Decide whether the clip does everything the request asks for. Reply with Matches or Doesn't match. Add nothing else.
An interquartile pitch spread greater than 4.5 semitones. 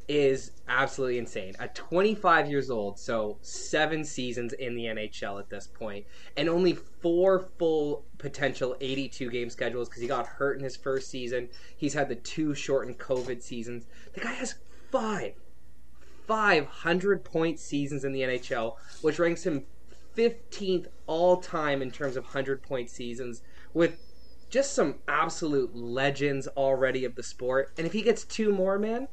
Matches